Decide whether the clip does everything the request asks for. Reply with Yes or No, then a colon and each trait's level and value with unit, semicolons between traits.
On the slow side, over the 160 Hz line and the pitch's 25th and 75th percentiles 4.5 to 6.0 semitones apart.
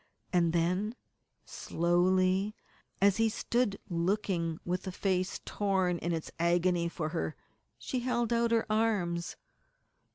No: slow, 125 wpm; medium, 185 Hz; average, 3.6 semitones